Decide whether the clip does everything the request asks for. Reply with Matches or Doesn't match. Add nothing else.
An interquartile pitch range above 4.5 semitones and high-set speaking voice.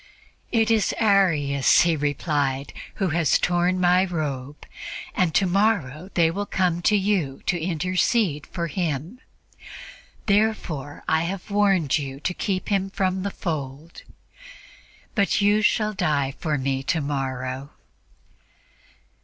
Doesn't match